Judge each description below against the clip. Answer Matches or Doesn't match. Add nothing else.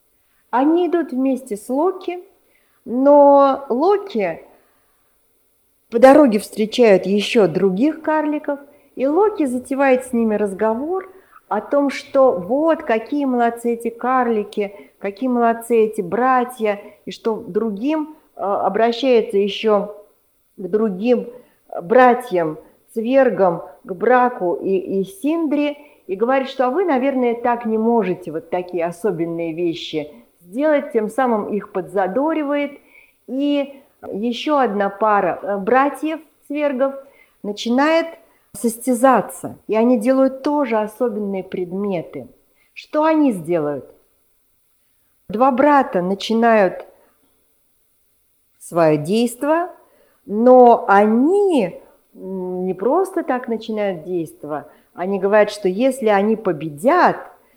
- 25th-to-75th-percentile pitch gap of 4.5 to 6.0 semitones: Matches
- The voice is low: Doesn't match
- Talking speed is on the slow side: Matches